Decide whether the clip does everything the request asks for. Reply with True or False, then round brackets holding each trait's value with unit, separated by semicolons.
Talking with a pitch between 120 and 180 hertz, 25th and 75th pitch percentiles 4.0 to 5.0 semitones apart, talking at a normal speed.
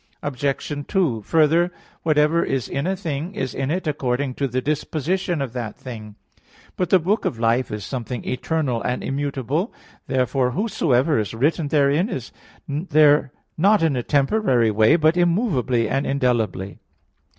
True (140 Hz; 4.7 semitones; 150 wpm)